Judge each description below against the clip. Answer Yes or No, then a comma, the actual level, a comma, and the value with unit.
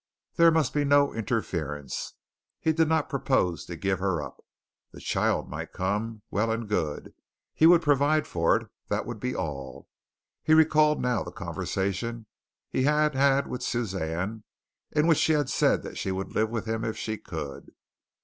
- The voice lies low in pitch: Yes, low, 115 Hz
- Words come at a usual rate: Yes, average, 175 wpm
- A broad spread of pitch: Yes, wide, 7.5 semitones